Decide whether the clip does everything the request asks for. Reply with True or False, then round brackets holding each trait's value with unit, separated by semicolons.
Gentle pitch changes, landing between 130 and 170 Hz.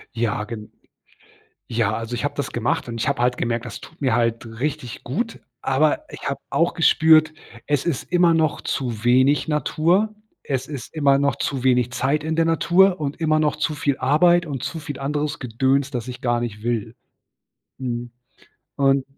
False (4.3 semitones; 140 Hz)